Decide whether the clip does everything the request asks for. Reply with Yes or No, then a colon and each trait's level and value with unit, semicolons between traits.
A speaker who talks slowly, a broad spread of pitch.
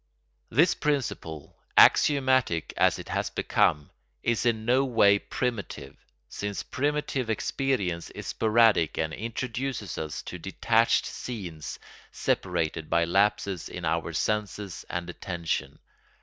Yes: slow, 115 wpm; wide, 6.6 semitones